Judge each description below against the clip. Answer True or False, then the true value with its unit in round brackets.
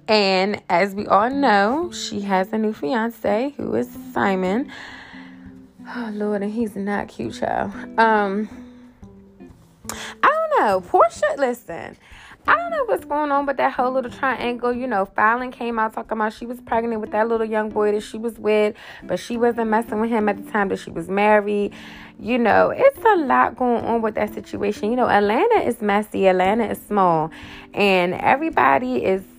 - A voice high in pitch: True (220 Hz)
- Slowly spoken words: False (185 wpm)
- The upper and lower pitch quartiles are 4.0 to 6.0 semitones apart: False (3.5 semitones)